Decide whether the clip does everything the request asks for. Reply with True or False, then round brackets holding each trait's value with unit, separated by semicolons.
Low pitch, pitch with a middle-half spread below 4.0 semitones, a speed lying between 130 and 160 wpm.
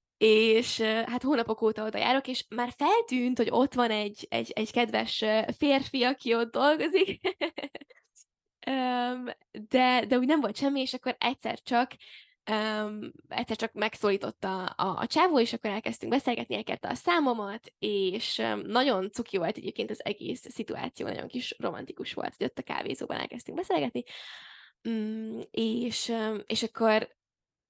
False (240 Hz; 2.9 semitones; 140 wpm)